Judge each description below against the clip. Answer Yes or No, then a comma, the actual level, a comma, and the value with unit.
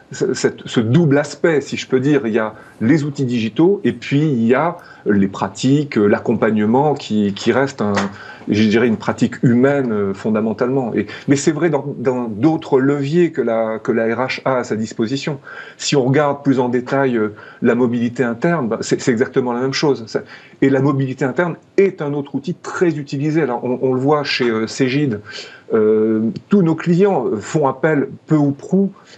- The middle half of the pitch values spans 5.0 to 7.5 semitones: No, average, 4.2 semitones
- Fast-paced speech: No, average, 185 wpm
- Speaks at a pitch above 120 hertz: Yes, low, 135 Hz